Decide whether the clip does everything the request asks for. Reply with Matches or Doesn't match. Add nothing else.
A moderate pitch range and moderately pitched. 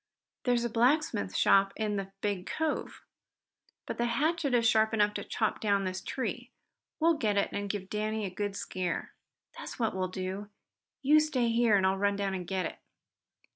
Doesn't match